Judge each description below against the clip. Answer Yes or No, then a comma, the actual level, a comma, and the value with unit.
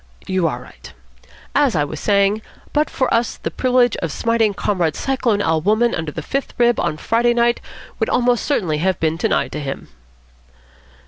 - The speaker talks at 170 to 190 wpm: Yes, average, 180 wpm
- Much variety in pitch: Yes, wide, 6.8 semitones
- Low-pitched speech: No, high, 210 Hz